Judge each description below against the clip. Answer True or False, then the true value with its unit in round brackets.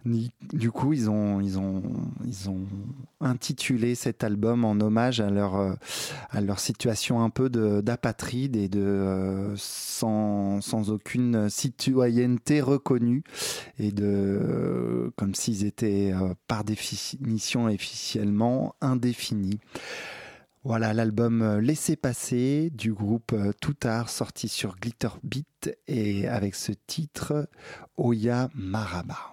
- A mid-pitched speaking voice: False (115 Hz)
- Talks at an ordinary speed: False (115 wpm)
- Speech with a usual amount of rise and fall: True (3.4 semitones)